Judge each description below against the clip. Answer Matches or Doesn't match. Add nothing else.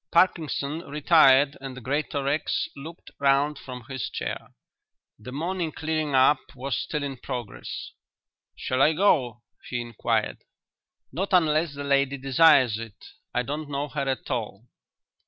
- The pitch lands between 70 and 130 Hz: Doesn't match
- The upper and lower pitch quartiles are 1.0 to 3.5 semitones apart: Matches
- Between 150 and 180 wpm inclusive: Doesn't match